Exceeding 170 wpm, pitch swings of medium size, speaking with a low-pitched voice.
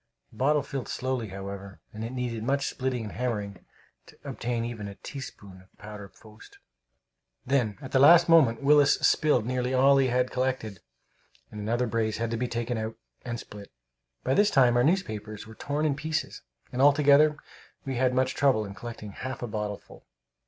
Yes: average, 185 wpm; average, 3.8 semitones; low, 125 Hz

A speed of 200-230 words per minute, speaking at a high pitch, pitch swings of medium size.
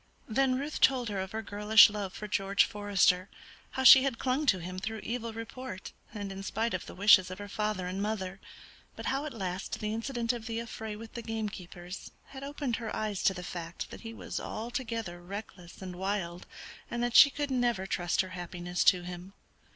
Yes: fast, 205 wpm; high, 210 Hz; average, 3.9 semitones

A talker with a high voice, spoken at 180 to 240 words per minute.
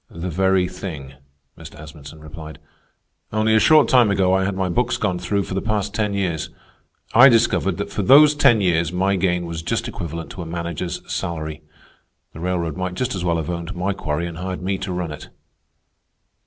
No: very low, 90 Hz; average, 195 wpm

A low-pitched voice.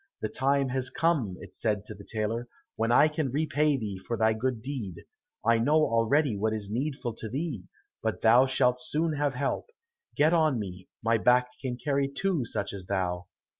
Yes: low, 125 Hz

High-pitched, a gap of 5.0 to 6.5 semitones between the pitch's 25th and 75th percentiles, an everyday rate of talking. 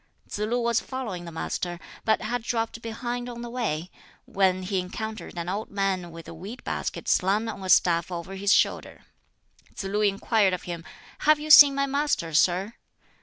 No: high, 200 Hz; average, 4.5 semitones; average, 185 wpm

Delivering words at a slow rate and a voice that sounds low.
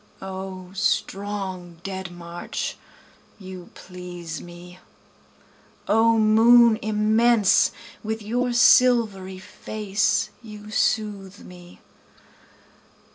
No: slow, 80 wpm; high, 200 Hz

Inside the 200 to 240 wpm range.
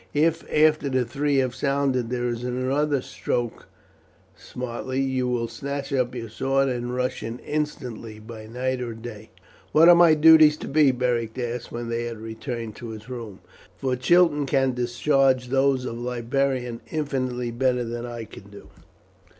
No: average, 165 wpm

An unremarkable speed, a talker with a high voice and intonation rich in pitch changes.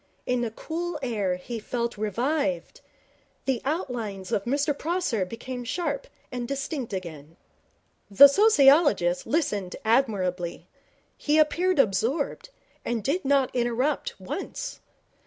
No: slow, 115 wpm; very high, 250 Hz; wide, 6.2 semitones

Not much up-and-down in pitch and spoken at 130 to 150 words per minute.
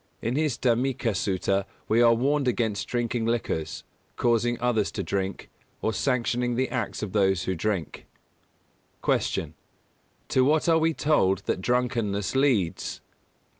No: average, 4.2 semitones; average, 140 wpm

